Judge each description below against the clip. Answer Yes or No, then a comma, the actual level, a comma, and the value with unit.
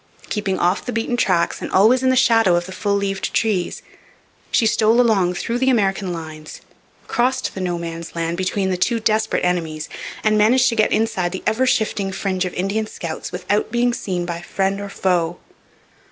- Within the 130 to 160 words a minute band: No, average, 190 wpm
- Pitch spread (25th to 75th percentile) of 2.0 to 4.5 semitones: Yes, average, 3.9 semitones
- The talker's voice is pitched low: No, high, 195 Hz